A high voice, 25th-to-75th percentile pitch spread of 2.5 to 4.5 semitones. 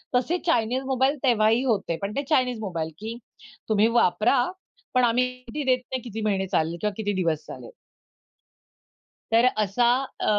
Yes: high, 230 Hz; average, 3.6 semitones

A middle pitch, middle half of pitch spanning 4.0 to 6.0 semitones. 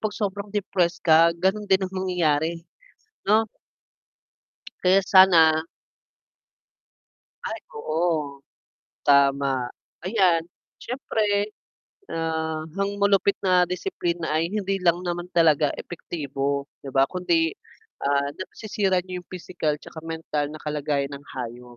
Yes: medium, 170 Hz; average, 4.3 semitones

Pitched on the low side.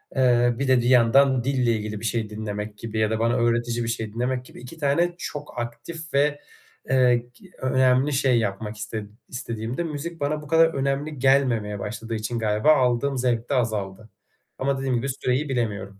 Yes: low, 125 Hz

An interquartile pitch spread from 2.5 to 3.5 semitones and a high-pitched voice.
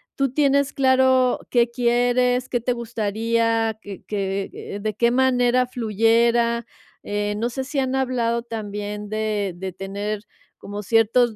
Yes: average, 3.0 semitones; high, 230 Hz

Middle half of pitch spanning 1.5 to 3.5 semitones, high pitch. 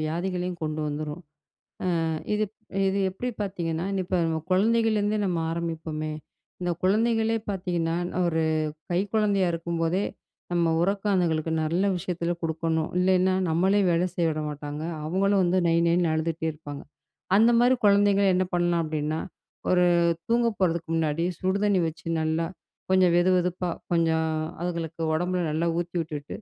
No: average, 2.8 semitones; medium, 175 Hz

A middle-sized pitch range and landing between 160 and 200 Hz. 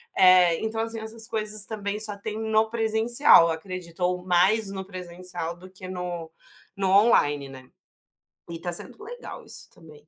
Yes: average, 4.0 semitones; high, 190 Hz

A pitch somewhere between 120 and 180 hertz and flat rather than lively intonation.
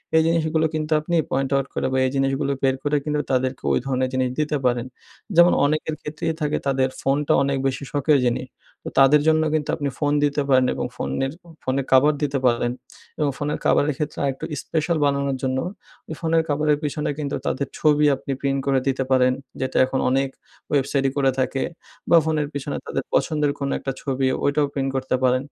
Yes: medium, 140 Hz; narrow, 2.1 semitones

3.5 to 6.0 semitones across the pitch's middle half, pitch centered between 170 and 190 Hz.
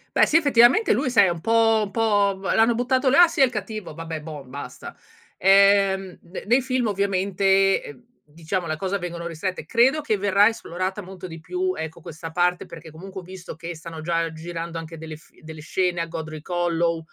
Yes: average, 4.1 semitones; medium, 185 Hz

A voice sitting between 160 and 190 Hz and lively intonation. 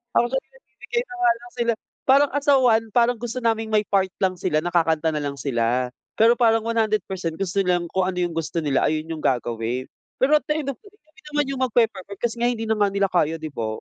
No: high, 200 Hz; wide, 6.9 semitones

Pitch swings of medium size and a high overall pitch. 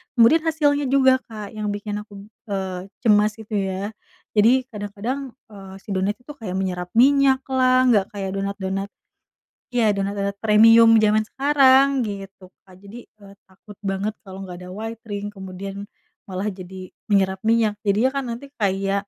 Yes: average, 3.0 semitones; high, 205 Hz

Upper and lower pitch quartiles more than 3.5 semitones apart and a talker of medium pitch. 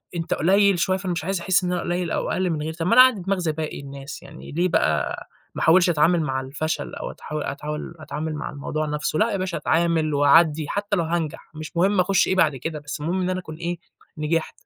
No: average, 3.2 semitones; medium, 165 Hz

